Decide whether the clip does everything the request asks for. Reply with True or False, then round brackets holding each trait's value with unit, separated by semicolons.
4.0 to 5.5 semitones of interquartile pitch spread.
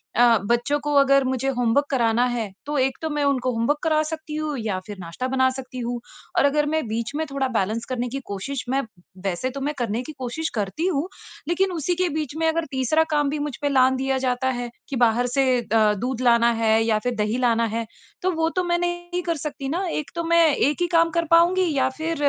True (4.5 semitones)